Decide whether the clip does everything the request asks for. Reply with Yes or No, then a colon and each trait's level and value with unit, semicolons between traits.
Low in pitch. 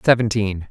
Yes: low, 105 Hz